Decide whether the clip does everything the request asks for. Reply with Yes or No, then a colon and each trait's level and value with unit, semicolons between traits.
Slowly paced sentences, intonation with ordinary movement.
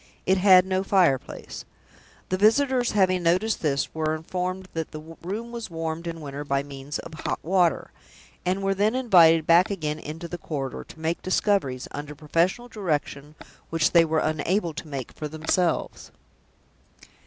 No: average, 165 wpm; average, 3.6 semitones